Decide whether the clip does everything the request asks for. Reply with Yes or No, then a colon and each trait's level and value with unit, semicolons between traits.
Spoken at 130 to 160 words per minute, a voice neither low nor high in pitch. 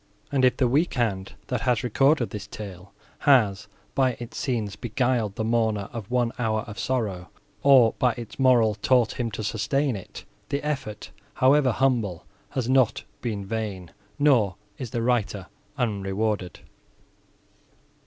No: average, 145 wpm; low, 115 Hz